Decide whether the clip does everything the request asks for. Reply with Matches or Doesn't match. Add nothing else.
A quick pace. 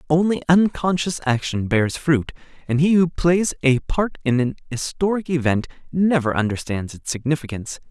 Doesn't match